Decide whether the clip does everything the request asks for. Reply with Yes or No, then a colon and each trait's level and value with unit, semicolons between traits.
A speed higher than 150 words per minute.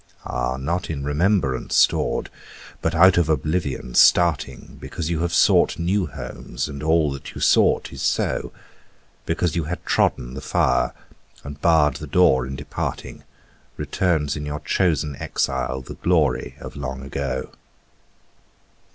No: average, 145 wpm